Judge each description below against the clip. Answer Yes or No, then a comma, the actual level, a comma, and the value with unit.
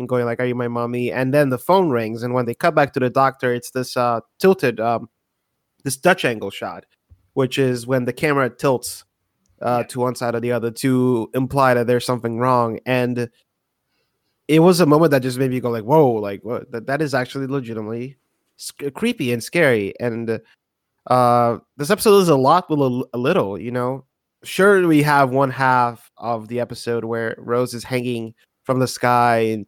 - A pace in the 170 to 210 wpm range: Yes, fast, 205 wpm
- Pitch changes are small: Yes, narrow, 2.3 semitones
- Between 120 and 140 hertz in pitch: Yes, low, 125 Hz